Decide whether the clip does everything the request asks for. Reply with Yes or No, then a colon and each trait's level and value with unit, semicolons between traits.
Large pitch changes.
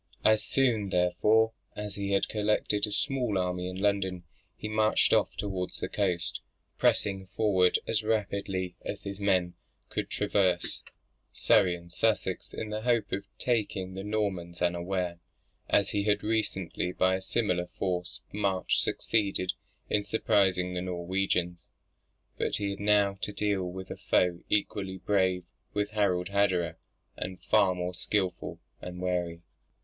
No: narrow, 2.4 semitones